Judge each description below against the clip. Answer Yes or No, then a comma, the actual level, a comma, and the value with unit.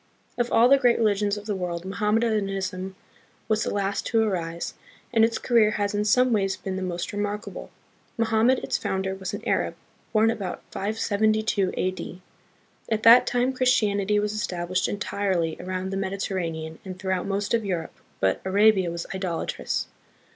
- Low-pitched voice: No, high, 200 Hz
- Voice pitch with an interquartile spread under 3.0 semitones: Yes, narrow, 2.6 semitones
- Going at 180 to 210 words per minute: No, average, 160 wpm